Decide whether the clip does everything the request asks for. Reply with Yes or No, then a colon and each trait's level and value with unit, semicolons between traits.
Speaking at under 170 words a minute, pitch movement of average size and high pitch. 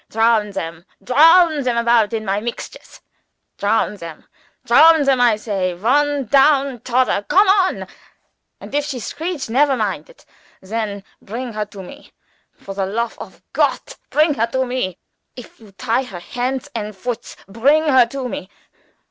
Yes: average, 155 wpm; average, 4.8 semitones; high, 235 Hz